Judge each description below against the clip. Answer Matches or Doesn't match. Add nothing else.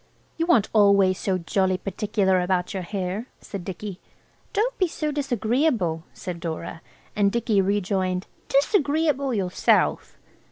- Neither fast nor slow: Doesn't match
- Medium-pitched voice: Doesn't match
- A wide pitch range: Matches